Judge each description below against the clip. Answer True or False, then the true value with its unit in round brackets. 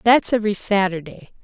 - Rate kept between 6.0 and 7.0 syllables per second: False (5.5 syllables/s)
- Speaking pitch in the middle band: False (205 Hz)